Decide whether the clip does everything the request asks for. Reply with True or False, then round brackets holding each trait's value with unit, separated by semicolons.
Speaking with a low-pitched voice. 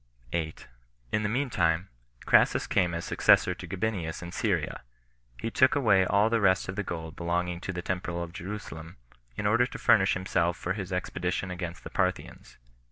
True (90 Hz)